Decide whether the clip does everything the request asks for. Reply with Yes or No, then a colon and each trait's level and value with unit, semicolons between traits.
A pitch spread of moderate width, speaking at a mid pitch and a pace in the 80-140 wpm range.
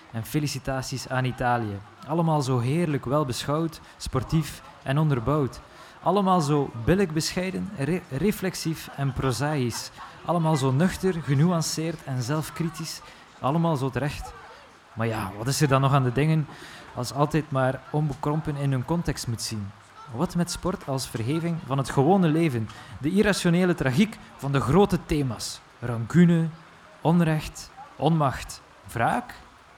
Yes: average, 4.1 semitones; medium, 150 Hz; slow, 135 wpm